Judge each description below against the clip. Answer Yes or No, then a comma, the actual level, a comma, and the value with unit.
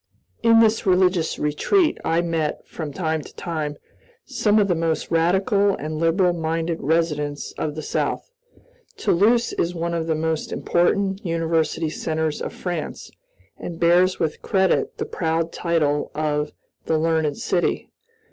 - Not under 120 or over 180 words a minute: Yes, average, 145 wpm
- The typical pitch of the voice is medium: Yes, medium, 165 Hz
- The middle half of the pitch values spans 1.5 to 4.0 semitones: Yes, narrow, 2.4 semitones